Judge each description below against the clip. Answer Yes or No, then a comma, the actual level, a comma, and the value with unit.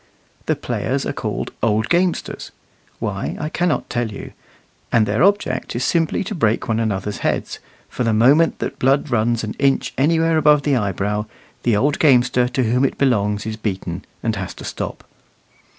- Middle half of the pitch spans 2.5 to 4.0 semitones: No, average, 5.1 semitones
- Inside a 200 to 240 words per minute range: No, average, 175 wpm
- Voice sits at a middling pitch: No, low, 120 Hz